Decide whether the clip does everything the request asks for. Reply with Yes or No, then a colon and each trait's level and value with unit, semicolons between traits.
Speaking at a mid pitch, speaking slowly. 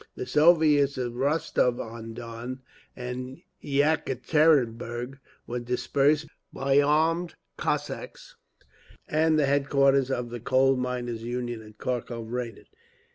No: low, 130 Hz; slow, 110 wpm